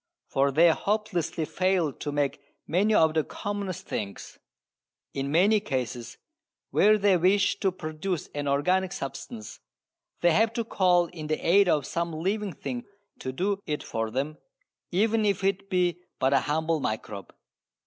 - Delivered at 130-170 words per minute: Yes, average, 155 wpm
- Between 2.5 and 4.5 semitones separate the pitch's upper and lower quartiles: No, average, 5.2 semitones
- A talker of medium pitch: Yes, medium, 170 Hz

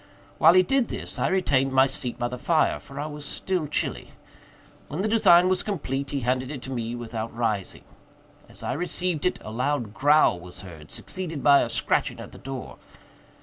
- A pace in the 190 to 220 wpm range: Yes, average, 195 wpm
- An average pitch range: No, wide, 5.9 semitones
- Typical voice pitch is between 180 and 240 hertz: No, medium, 140 Hz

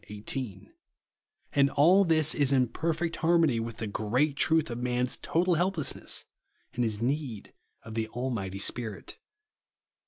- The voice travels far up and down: Yes, wide, 5.8 semitones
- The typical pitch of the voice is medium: No, low, 130 Hz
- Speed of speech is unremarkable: Yes, average, 150 wpm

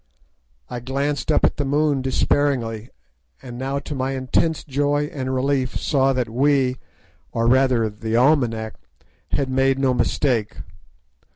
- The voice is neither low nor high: No, low, 130 Hz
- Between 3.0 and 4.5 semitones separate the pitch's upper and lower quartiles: No, narrow, 2.4 semitones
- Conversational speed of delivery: No, slow, 125 wpm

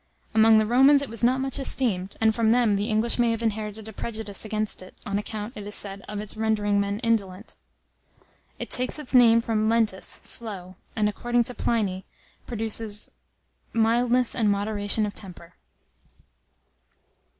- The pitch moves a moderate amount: No, narrow, 2.2 semitones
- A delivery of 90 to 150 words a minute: No, average, 160 wpm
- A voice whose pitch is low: No, high, 220 Hz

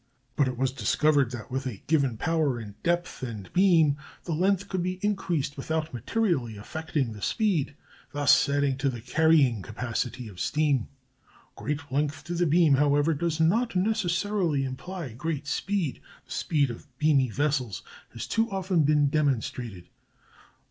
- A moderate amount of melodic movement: Yes, average, 4.7 semitones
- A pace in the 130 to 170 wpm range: Yes, average, 150 wpm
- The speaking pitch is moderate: Yes, medium, 145 Hz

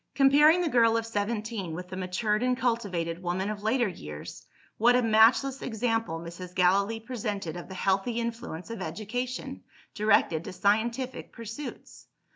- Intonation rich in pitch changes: No, average, 4.3 semitones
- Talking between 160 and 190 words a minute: No, average, 150 wpm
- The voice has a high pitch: Yes, high, 220 Hz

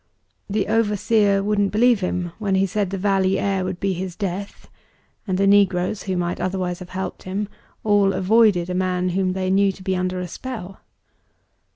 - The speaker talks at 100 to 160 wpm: No, average, 185 wpm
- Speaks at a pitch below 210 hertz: Yes, high, 190 Hz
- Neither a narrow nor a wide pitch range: No, narrow, 1.8 semitones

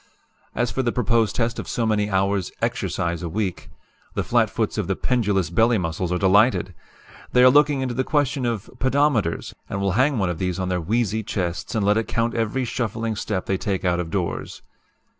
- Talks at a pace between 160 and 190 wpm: No, fast, 205 wpm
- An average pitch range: Yes, average, 4.5 semitones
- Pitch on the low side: Yes, low, 105 Hz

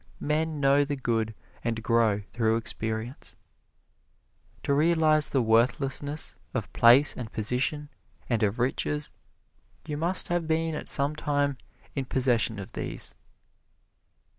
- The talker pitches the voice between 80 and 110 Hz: No, low, 135 Hz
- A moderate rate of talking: No, slow, 125 wpm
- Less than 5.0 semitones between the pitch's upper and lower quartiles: Yes, average, 4.6 semitones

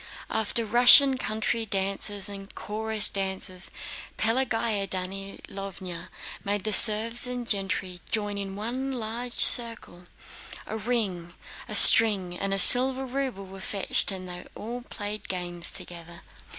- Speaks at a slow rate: Yes, slow, 125 wpm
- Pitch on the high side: Yes, high, 205 Hz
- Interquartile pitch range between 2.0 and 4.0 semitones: Yes, average, 3.3 semitones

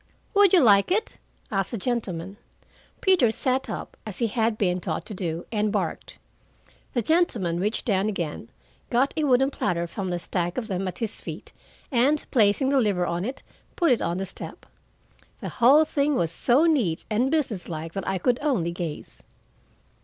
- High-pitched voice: Yes, high, 215 Hz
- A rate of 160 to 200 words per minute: Yes, average, 180 wpm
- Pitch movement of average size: No, wide, 6.7 semitones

